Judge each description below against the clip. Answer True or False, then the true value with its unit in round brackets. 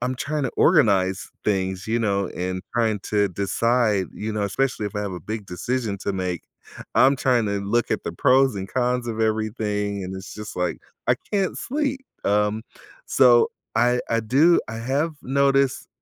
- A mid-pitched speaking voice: False (110 Hz)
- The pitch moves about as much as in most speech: True (4.2 semitones)